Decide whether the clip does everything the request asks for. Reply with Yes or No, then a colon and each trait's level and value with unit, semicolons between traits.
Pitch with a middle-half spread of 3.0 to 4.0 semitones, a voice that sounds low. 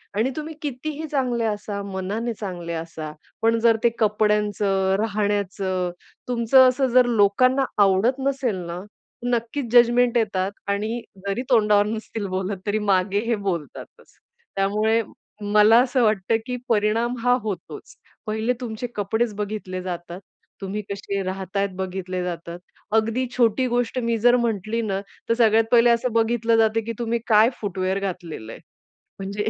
No: average, 3.3 semitones; high, 215 Hz